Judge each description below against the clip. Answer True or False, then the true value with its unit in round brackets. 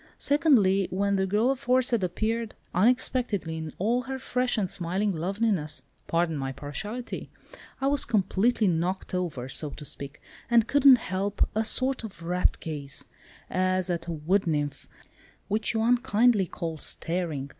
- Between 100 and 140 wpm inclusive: True (135 wpm)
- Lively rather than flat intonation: True (5.9 semitones)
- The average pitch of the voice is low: False (195 Hz)